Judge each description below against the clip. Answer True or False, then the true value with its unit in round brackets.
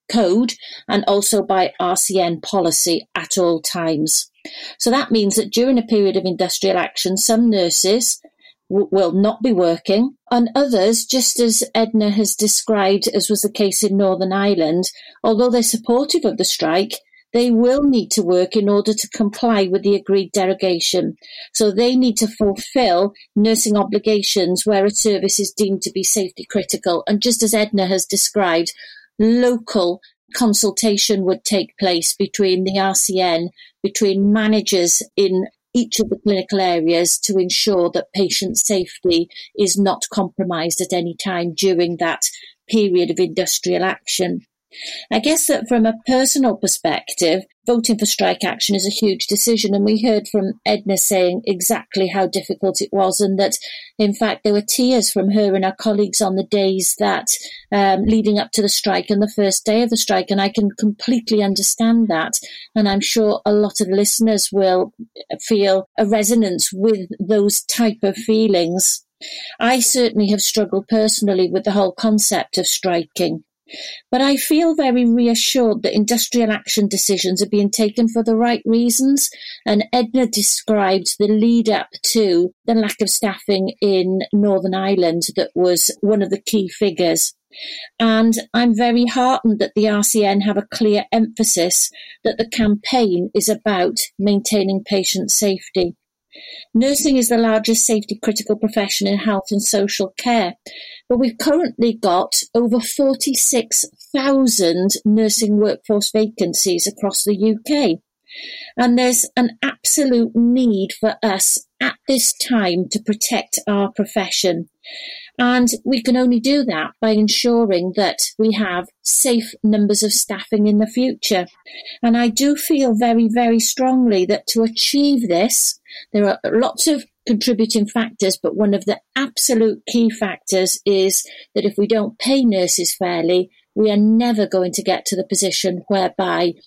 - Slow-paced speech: False (155 wpm)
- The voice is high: True (210 Hz)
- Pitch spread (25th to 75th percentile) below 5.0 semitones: True (3.2 semitones)